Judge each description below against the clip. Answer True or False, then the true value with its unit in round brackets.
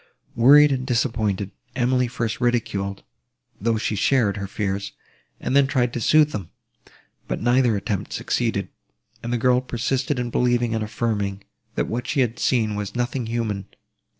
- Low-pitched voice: True (120 Hz)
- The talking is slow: False (155 wpm)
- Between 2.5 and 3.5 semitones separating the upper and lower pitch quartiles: True (3.1 semitones)